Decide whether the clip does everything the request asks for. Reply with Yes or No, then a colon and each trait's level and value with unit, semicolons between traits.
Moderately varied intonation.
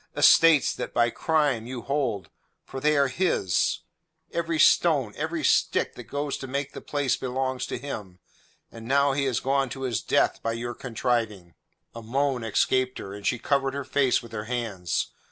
Yes: average, 3.5 semitones